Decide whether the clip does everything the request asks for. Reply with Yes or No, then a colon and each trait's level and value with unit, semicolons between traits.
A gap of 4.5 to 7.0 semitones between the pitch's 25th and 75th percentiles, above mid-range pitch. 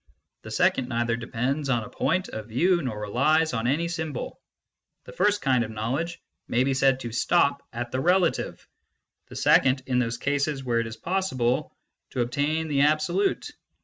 No: average, 4.9 semitones; low, 135 Hz